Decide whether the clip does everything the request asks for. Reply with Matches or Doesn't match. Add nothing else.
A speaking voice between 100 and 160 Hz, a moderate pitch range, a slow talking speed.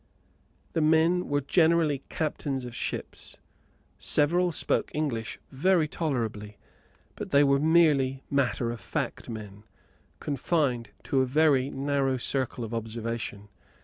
Matches